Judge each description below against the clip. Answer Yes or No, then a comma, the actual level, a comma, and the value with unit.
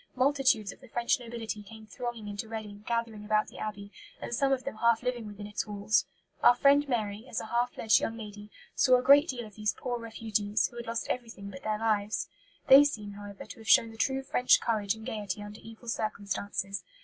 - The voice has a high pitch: Yes, high, 225 Hz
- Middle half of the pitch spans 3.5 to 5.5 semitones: No, narrow, 2.6 semitones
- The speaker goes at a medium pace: No, fast, 215 wpm